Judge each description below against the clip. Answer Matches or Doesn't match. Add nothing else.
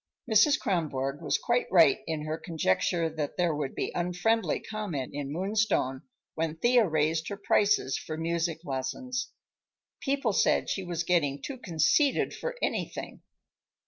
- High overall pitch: Doesn't match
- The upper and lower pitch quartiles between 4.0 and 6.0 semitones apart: Matches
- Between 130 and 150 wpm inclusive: Matches